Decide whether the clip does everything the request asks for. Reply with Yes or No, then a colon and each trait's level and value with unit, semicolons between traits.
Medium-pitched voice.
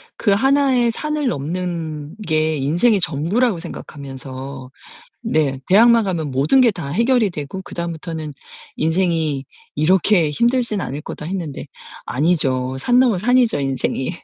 Yes: medium, 170 Hz